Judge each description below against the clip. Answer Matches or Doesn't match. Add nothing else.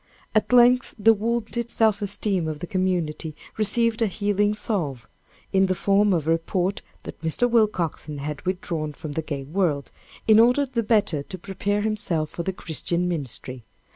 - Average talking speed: Matches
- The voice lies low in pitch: Doesn't match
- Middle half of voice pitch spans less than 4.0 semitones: Doesn't match